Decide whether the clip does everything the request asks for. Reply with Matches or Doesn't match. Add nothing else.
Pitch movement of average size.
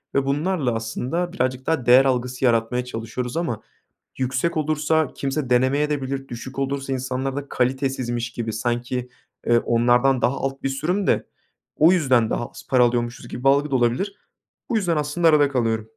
Matches